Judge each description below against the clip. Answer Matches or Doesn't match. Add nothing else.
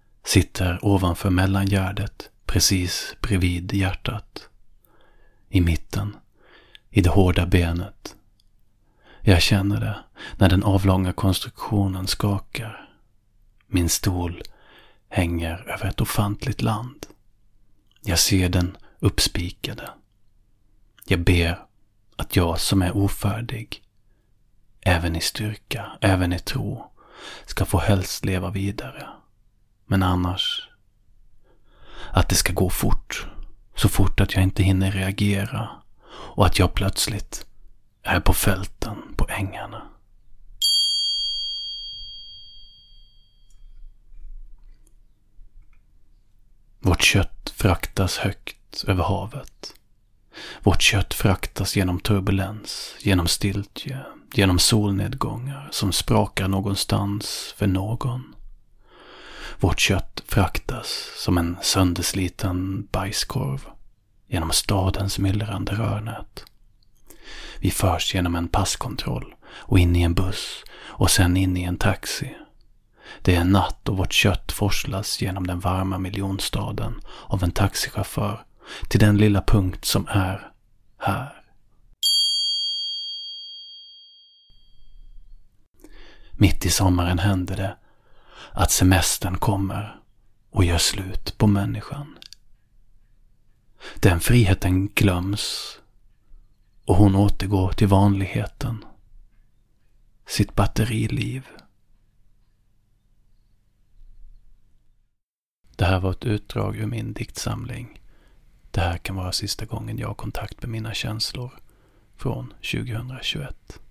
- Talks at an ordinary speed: Doesn't match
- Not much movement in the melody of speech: Matches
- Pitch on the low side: Matches